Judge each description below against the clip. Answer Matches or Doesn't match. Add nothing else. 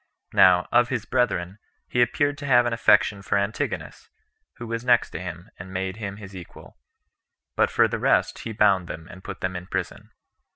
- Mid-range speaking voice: Doesn't match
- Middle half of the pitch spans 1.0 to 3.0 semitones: Doesn't match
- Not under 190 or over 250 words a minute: Matches